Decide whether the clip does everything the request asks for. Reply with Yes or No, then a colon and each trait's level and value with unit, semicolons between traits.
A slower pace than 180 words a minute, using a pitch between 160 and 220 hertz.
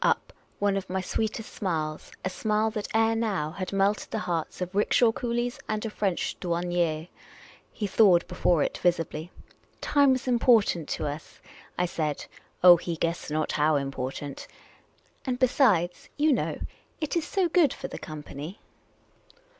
Yes: average, 170 wpm; medium, 185 Hz